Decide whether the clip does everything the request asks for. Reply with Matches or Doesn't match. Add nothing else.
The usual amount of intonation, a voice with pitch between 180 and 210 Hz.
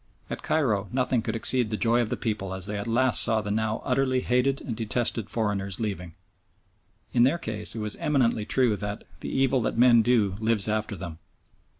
Doesn't match